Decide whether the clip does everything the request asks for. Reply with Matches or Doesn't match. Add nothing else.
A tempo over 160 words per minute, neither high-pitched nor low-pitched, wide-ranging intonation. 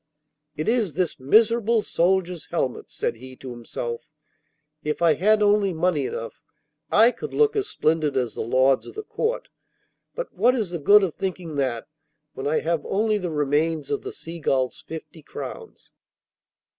Matches